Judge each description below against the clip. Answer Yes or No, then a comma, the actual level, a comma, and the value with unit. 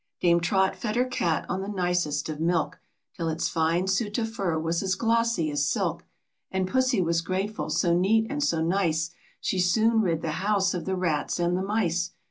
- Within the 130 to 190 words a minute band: No, average, 200 wpm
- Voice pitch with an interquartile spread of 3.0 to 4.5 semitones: Yes, average, 3.8 semitones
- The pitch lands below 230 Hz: Yes, medium, 185 Hz